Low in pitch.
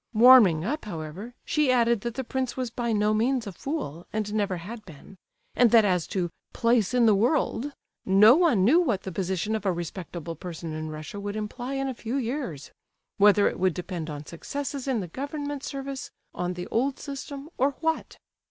No: high, 220 Hz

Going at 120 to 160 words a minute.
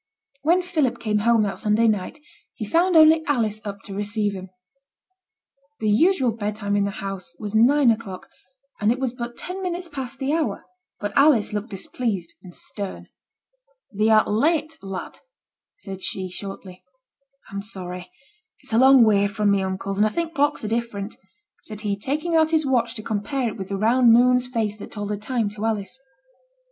No: average, 180 wpm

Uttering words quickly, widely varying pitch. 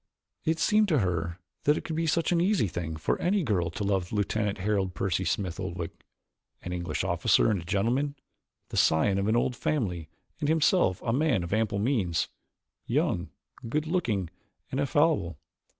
No: average, 175 wpm; wide, 8.7 semitones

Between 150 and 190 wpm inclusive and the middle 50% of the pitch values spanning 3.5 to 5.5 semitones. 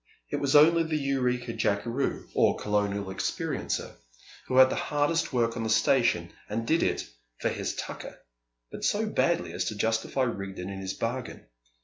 Yes: average, 165 wpm; average, 5.2 semitones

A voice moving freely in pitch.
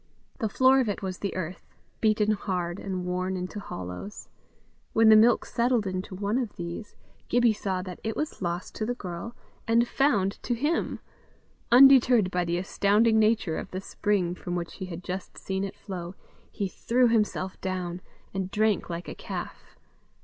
No: average, 3.7 semitones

